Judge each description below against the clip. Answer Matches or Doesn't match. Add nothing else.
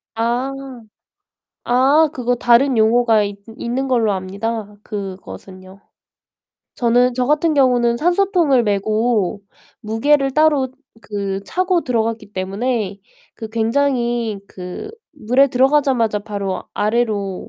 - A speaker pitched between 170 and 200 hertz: Doesn't match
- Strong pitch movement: Doesn't match